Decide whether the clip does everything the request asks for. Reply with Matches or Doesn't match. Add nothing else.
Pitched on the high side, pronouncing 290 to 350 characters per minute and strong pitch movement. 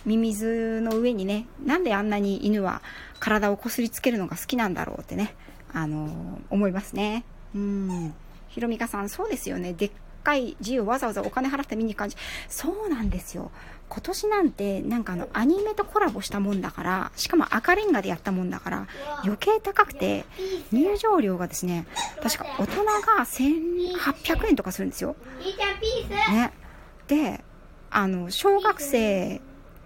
Matches